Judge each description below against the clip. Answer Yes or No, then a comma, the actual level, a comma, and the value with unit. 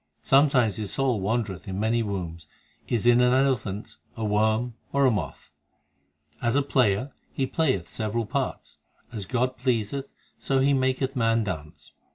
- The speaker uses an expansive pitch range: No, average, 4.0 semitones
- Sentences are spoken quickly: No, average, 160 wpm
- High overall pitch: No, low, 115 Hz